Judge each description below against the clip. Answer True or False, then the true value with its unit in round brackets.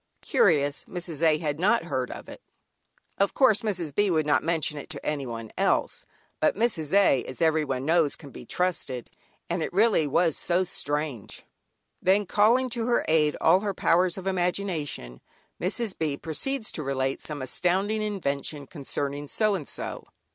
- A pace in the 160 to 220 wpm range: True (170 wpm)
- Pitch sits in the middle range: True (165 Hz)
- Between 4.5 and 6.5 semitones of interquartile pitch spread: True (5.2 semitones)